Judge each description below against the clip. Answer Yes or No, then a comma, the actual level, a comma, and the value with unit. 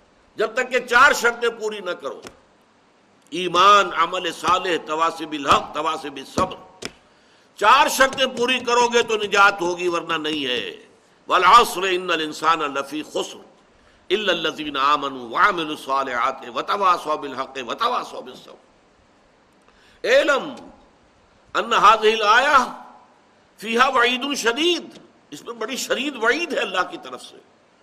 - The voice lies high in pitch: Yes, high, 210 Hz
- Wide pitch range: Yes, wide, 8.1 semitones